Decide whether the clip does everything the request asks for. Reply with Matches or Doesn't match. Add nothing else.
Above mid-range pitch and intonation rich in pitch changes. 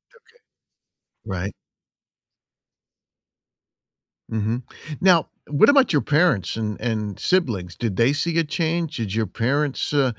Doesn't match